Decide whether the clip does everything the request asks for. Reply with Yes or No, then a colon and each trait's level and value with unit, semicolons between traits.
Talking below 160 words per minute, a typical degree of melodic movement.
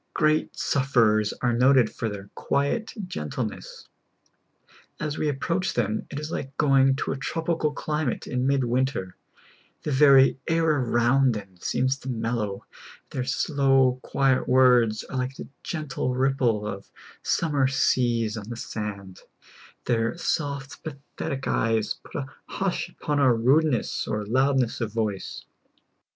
Yes: average, 140 wpm; average, 3.7 semitones